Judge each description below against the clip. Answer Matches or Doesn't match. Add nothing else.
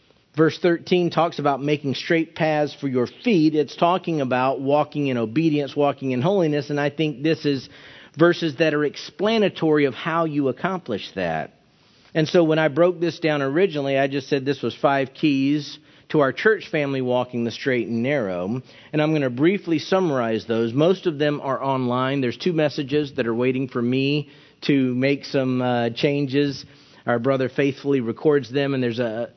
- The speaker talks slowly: Doesn't match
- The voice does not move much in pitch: Doesn't match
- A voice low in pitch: Doesn't match